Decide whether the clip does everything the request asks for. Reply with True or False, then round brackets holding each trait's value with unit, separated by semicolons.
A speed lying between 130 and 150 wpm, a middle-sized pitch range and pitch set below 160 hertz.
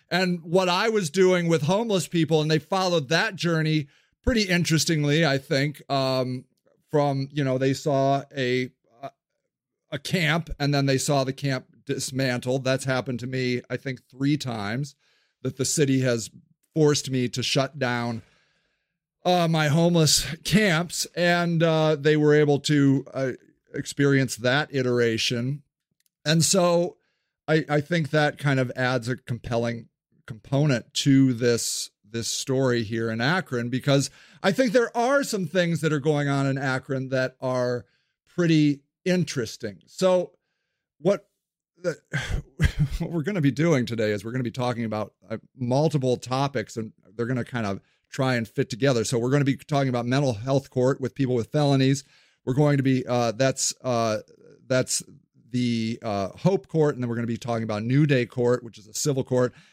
False (170 wpm; 4.1 semitones; 135 Hz)